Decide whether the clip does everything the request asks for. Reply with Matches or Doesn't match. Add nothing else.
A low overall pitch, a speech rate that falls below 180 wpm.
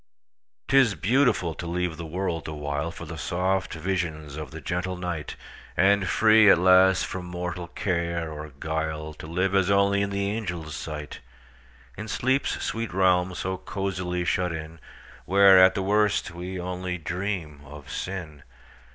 Matches